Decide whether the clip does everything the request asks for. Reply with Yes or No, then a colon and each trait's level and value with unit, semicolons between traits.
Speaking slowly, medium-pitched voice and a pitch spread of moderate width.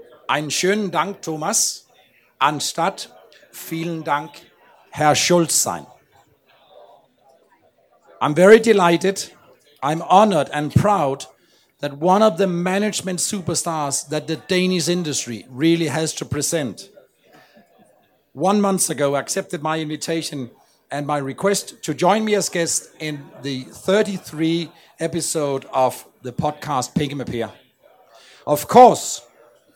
Yes: slow, 105 wpm; medium, 160 Hz; average, 4.2 semitones